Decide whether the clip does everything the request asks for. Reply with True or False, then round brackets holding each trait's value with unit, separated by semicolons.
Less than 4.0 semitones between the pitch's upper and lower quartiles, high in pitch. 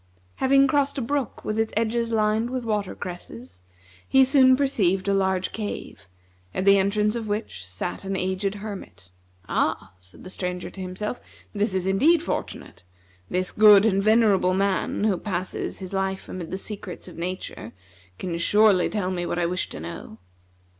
True (3.1 semitones; 195 Hz)